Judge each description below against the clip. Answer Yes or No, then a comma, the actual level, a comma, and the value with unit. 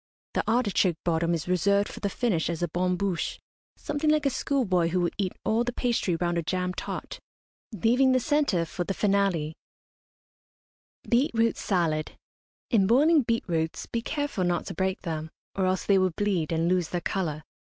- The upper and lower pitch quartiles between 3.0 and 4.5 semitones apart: No, average, 5.1 semitones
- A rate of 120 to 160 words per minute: No, average, 180 wpm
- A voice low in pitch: No, high, 190 Hz